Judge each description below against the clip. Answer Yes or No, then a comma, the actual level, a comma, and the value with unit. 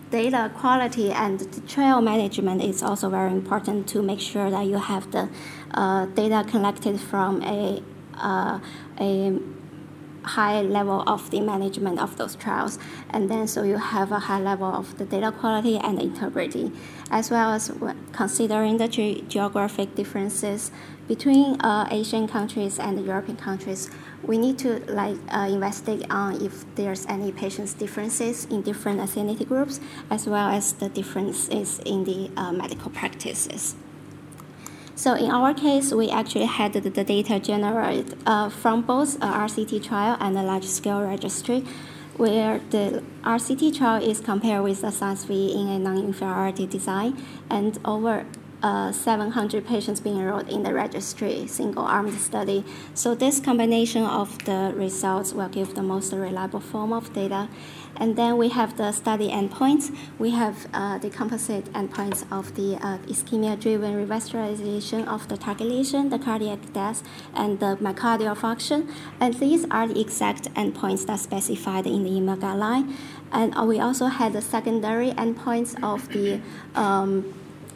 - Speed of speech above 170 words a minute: No, average, 155 wpm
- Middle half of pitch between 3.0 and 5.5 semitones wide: No, narrow, 2.5 semitones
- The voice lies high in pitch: Yes, high, 210 Hz